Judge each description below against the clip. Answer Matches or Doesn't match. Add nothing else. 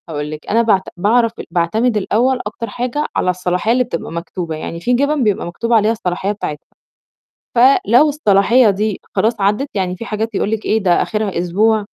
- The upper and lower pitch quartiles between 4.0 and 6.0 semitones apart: Matches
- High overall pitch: Matches